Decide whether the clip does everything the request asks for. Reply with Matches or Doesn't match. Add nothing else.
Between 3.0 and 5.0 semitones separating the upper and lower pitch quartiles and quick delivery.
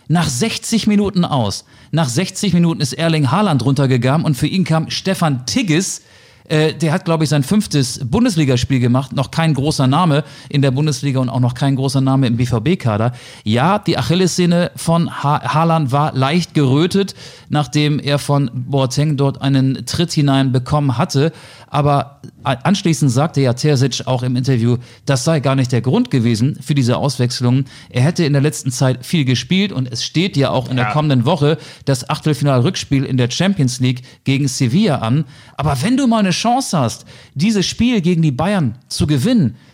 Doesn't match